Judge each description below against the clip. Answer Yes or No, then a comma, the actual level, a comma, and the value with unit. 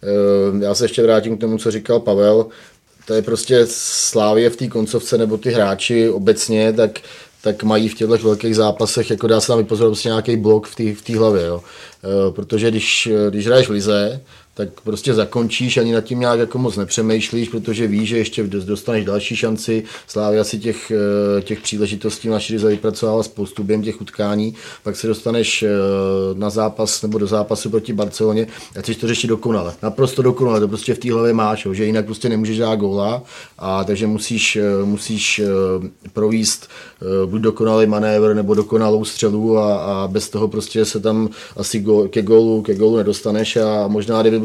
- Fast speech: Yes, fast, 180 wpm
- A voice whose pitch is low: Yes, low, 110 Hz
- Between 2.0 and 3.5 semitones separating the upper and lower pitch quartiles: No, narrow, 1.4 semitones